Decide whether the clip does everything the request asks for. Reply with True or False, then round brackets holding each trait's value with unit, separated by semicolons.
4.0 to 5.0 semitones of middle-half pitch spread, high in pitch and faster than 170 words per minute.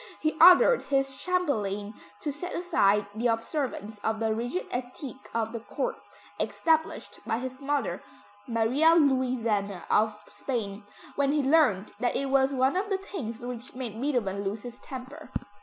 False (4.7 semitones; 250 Hz; 155 wpm)